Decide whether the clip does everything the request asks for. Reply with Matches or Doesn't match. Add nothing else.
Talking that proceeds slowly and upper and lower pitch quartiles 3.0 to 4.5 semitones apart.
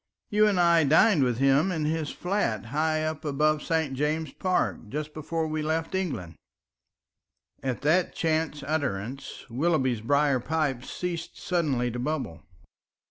Doesn't match